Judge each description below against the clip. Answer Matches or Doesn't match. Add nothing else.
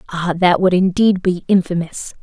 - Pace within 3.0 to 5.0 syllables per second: Matches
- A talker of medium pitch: Matches